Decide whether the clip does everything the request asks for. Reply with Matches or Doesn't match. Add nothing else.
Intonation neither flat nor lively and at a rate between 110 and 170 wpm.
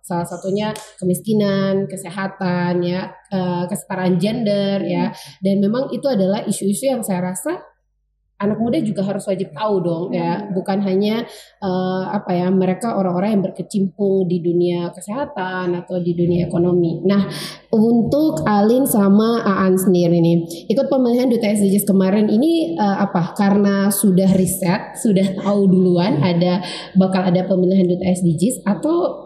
Doesn't match